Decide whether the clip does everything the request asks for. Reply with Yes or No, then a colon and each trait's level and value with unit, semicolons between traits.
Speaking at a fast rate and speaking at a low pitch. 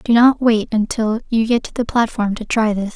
No: fast, 245 wpm; high, 225 Hz